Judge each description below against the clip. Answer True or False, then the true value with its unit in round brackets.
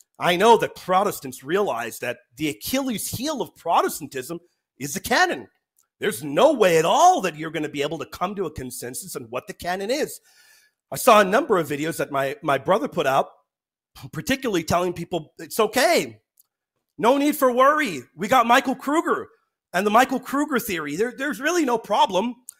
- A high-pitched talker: True (210 Hz)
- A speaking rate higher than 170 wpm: True (185 wpm)